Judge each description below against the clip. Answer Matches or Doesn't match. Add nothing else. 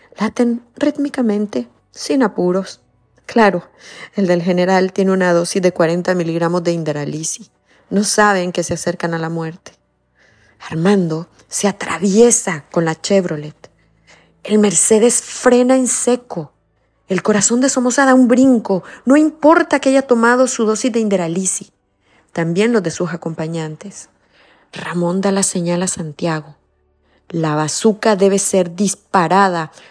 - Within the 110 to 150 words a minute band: Matches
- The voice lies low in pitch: Doesn't match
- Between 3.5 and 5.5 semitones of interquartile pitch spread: Matches